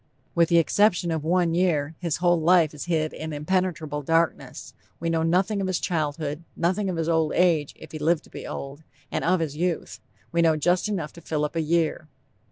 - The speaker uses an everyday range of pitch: No, narrow, 2.3 semitones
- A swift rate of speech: Yes, fast, 210 wpm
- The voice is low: No, medium, 165 Hz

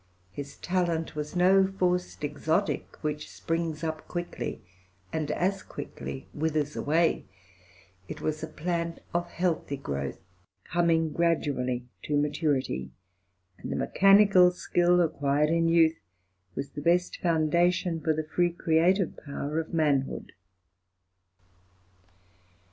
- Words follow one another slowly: Yes, slow, 115 wpm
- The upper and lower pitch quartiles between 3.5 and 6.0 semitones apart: No, average, 2.7 semitones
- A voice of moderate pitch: Yes, medium, 160 Hz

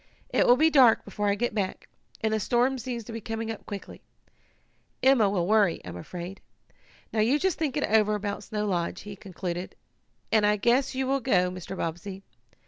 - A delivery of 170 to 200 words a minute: Yes, average, 195 wpm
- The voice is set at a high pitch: Yes, high, 215 Hz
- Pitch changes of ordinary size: Yes, average, 3.8 semitones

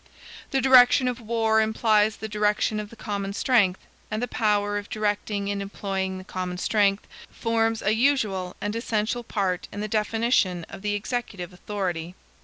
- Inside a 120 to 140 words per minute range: No, average, 165 wpm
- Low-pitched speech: No, high, 210 Hz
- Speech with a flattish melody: Yes, narrow, 2.3 semitones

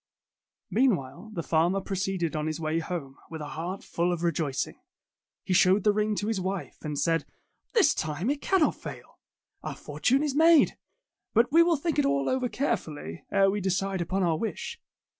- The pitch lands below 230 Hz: Yes, high, 190 Hz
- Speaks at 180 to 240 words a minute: Yes, average, 185 wpm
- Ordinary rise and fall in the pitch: No, wide, 6.0 semitones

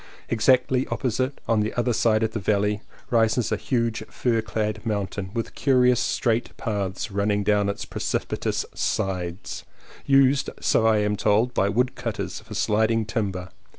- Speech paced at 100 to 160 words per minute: Yes, average, 150 wpm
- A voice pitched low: Yes, low, 110 Hz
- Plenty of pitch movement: No, average, 2.8 semitones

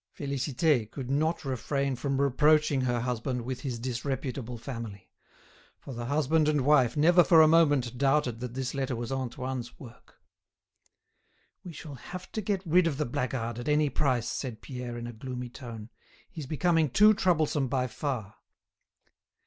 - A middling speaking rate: Yes, average, 160 wpm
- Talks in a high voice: No, low, 135 Hz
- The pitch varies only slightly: No, average, 3.7 semitones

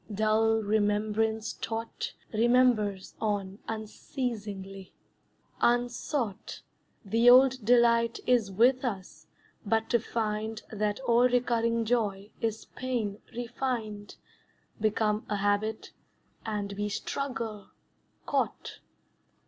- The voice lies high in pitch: Yes, high, 220 Hz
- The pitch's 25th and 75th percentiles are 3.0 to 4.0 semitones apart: No, narrow, 2.4 semitones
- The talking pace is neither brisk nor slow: No, slow, 90 wpm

